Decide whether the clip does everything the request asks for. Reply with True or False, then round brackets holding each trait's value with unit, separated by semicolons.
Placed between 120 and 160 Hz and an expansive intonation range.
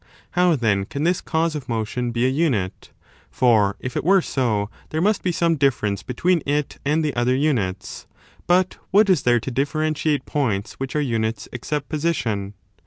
True (135 Hz; 5.8 semitones)